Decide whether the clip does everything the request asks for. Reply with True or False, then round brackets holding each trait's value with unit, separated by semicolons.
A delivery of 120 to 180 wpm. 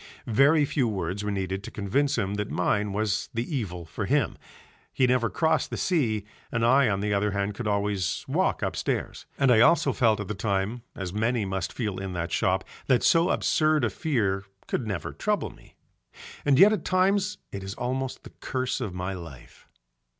False (195 wpm)